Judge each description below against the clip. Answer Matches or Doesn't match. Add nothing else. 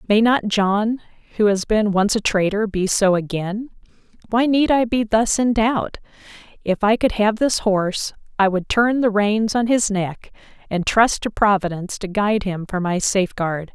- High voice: Matches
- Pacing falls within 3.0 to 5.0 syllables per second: Matches